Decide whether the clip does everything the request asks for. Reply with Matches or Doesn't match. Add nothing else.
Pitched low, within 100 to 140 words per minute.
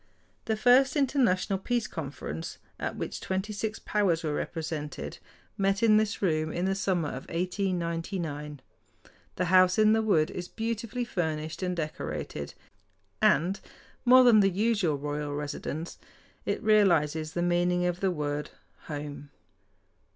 Doesn't match